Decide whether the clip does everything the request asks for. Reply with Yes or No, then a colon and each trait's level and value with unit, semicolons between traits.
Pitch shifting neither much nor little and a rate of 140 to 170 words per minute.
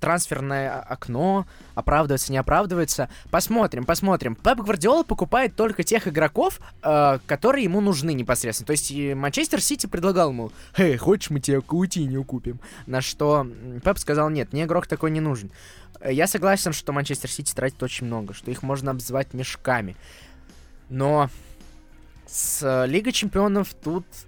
No: wide, 6.0 semitones; average, 150 wpm